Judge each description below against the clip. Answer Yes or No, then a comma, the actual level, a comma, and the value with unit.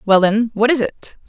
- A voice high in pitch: Yes, high, 220 Hz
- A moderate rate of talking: No, fast, 235 wpm